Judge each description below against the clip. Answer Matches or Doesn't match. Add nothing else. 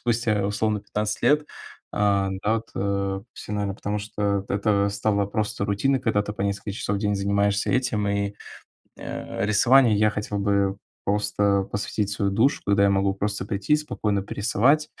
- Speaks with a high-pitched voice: Doesn't match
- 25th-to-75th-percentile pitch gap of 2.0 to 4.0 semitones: Doesn't match